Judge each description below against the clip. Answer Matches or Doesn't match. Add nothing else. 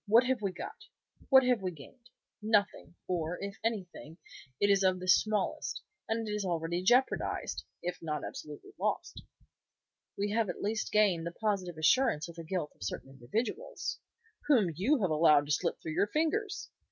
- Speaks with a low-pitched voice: Doesn't match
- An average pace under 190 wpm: Matches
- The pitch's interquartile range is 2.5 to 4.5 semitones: Doesn't match